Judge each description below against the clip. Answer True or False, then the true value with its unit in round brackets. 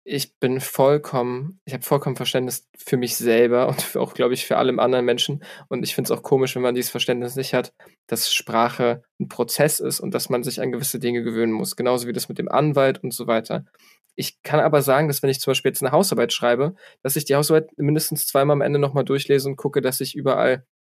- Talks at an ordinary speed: False (235 wpm)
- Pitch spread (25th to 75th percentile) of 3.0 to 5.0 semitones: False (2.5 semitones)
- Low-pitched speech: True (130 Hz)